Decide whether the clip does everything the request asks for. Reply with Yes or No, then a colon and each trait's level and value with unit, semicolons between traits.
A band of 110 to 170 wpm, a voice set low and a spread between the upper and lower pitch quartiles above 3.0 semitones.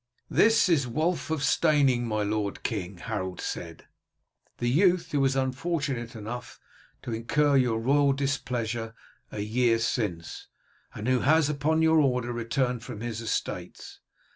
Yes: average, 140 wpm; low, 125 Hz; average, 4.2 semitones